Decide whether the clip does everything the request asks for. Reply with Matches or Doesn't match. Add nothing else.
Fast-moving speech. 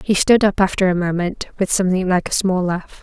Matches